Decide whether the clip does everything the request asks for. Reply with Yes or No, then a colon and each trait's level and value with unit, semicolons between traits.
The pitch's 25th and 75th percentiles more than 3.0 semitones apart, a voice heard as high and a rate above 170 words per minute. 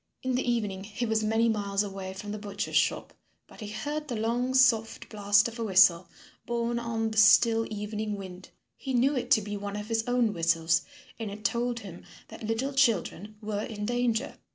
No: narrow, 2.5 semitones; high, 220 Hz; average, 200 wpm